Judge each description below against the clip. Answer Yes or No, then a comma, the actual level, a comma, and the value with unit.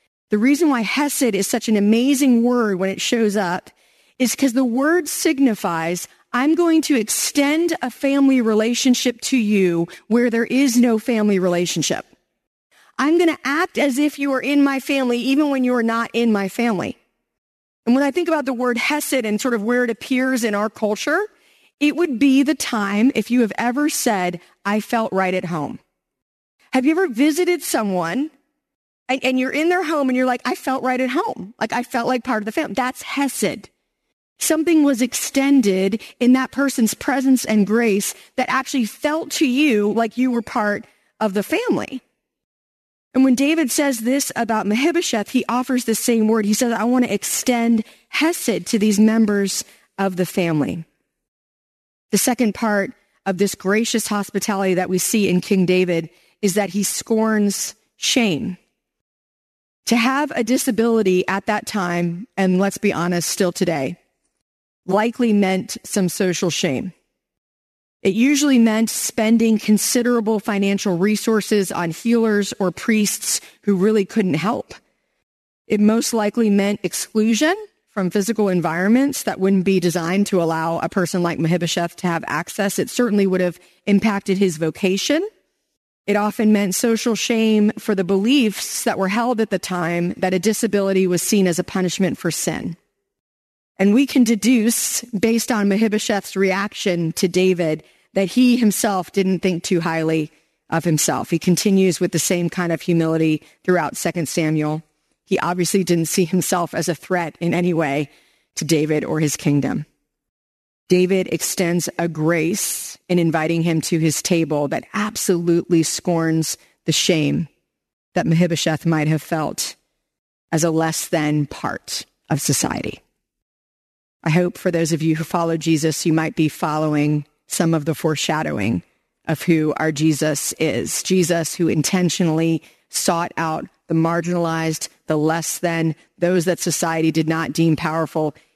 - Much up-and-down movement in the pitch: Yes, wide, 6.1 semitones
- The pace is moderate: Yes, average, 160 wpm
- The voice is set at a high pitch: Yes, high, 205 Hz